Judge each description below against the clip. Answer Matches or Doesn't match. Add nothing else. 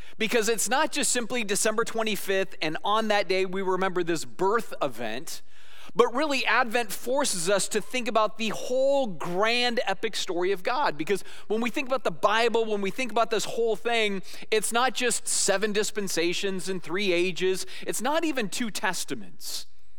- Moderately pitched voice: Doesn't match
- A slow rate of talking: Doesn't match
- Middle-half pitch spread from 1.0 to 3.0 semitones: Doesn't match